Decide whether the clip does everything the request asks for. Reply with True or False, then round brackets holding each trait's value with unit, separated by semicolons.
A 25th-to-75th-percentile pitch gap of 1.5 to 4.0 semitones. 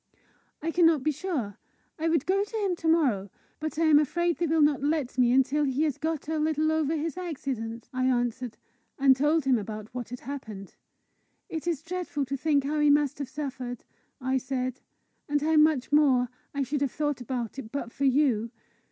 True (3.5 semitones)